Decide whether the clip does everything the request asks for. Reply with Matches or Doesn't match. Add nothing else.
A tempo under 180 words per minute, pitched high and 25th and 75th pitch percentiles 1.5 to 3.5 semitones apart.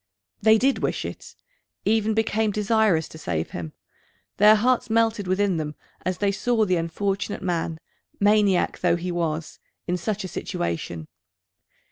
Doesn't match